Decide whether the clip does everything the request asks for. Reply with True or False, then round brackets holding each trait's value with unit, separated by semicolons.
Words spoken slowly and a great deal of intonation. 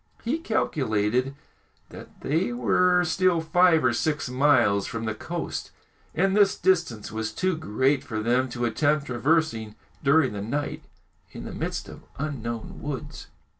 False (145 wpm; 6.0 semitones)